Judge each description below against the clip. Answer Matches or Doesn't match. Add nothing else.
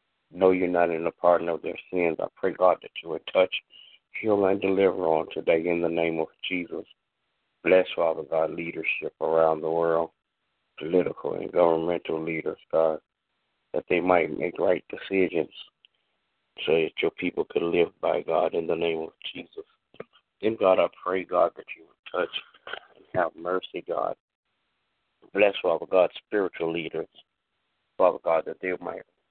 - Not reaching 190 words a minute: Matches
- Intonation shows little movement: Matches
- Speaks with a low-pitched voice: Matches